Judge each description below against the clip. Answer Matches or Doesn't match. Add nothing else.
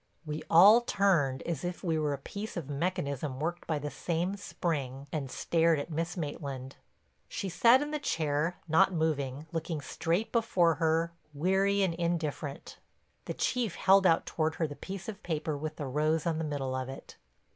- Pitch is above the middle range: Doesn't match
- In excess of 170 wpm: Matches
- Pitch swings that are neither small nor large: Matches